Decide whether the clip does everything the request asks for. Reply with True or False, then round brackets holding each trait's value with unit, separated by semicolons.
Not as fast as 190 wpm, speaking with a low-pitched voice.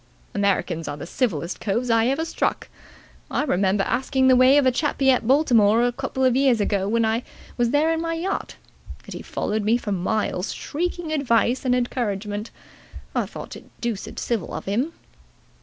False (180 wpm; 240 Hz)